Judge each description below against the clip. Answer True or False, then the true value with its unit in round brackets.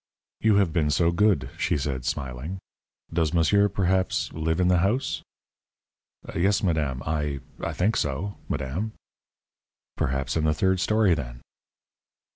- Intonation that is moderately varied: True (4.9 semitones)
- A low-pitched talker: True (85 Hz)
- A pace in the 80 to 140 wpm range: True (135 wpm)